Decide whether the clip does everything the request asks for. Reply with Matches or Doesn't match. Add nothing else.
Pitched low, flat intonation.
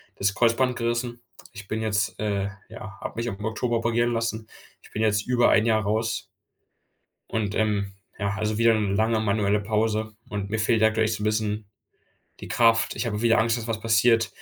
Matches